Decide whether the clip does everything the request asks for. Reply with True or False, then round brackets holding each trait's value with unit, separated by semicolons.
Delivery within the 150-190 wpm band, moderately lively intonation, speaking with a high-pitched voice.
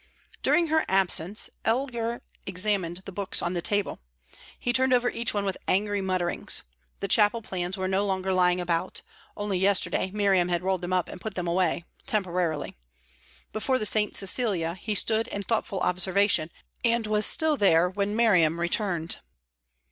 True (165 wpm; 3.0 semitones; 195 Hz)